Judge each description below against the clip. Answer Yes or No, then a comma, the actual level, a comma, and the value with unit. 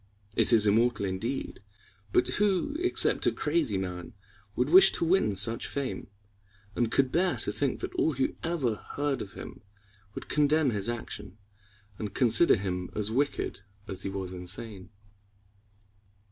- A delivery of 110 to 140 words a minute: No, average, 150 wpm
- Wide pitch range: Yes, wide, 6.5 semitones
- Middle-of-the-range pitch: No, low, 120 Hz